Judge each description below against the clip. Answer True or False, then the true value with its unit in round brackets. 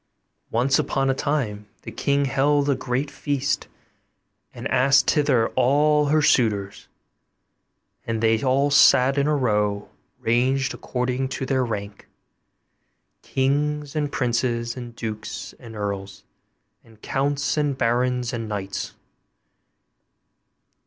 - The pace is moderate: False (120 wpm)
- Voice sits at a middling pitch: False (130 Hz)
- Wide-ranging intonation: False (3.7 semitones)